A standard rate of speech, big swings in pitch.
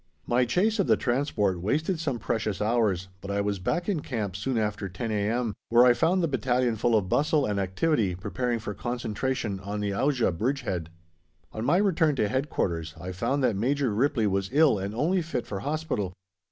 Yes: average, 195 wpm; wide, 5.7 semitones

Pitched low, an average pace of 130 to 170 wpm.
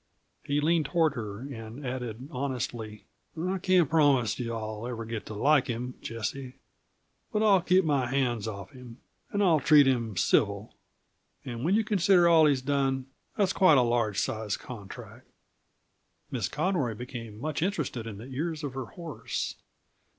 Yes: low, 130 Hz; average, 160 wpm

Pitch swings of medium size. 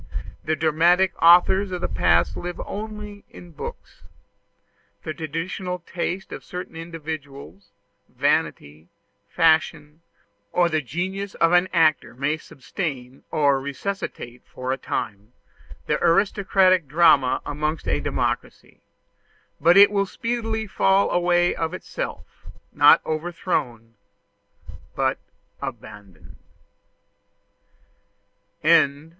Yes: average, 4.7 semitones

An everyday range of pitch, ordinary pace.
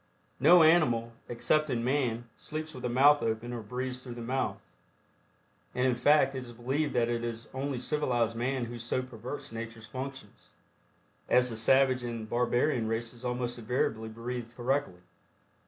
No: narrow, 2.2 semitones; average, 155 wpm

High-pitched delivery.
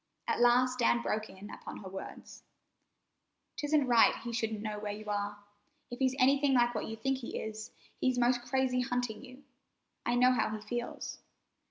Yes: high, 240 Hz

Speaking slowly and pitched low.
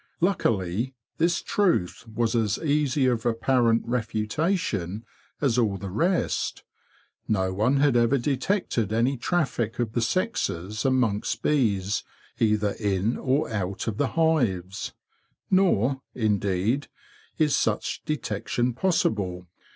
Yes: slow, 115 wpm; low, 115 Hz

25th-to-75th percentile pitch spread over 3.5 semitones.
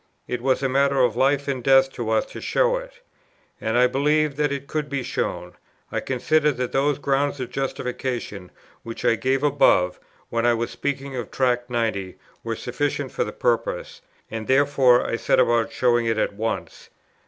No: average, 3.0 semitones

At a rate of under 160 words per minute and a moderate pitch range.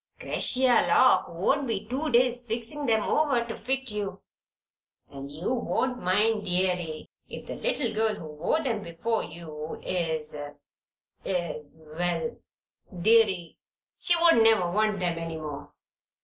No: slow, 135 wpm; wide, 6.1 semitones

